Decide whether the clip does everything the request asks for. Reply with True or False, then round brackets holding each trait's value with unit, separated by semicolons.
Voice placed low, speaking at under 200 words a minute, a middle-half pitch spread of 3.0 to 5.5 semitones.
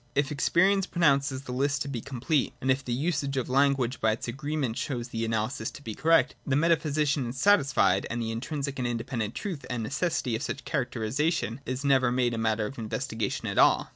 False (130 Hz; 205 wpm; 3.6 semitones)